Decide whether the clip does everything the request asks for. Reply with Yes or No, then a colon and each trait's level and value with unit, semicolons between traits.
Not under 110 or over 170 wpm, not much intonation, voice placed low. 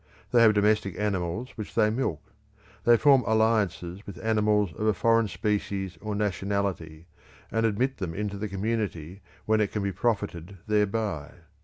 Yes: average, 155 wpm; narrow, 2.3 semitones; low, 105 Hz